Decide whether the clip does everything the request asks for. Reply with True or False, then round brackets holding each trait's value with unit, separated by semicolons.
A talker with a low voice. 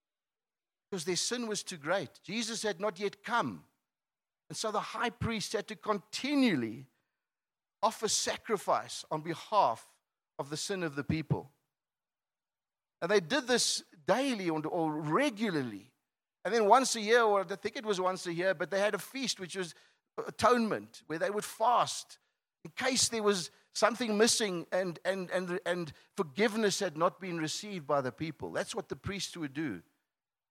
False (200 Hz)